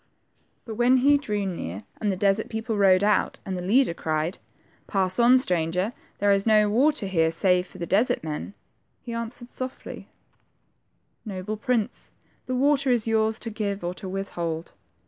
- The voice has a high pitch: Yes, high, 205 Hz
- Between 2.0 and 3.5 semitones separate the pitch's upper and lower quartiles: No, average, 4.4 semitones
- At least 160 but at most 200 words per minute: Yes, average, 175 wpm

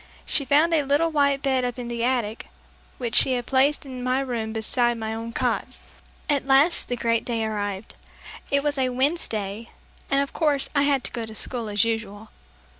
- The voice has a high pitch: Yes, very high, 250 Hz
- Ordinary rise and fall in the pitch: Yes, average, 3.7 semitones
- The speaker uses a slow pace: No, average, 190 wpm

